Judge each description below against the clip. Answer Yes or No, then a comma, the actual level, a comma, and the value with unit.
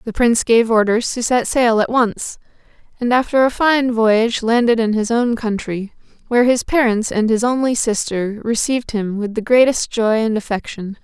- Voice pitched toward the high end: Yes, high, 230 Hz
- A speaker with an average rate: Yes, average, 185 wpm